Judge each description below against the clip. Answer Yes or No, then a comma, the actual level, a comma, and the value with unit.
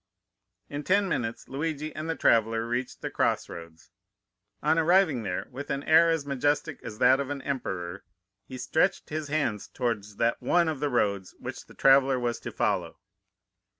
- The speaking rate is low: No, average, 175 wpm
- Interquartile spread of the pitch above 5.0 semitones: Yes, wide, 5.5 semitones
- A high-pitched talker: No, low, 135 Hz